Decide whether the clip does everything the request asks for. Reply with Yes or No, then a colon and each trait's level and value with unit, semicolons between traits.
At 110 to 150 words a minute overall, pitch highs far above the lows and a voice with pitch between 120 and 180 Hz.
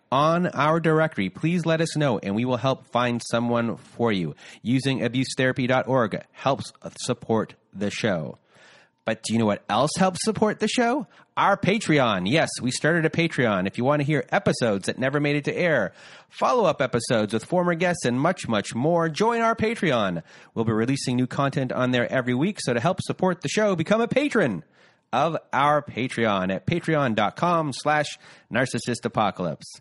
No: average, 175 wpm; wide, 5.7 semitones; medium, 140 Hz